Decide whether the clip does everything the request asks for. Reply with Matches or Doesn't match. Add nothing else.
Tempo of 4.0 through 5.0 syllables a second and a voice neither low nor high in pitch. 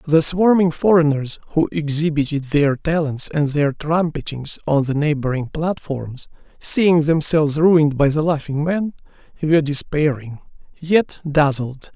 Matches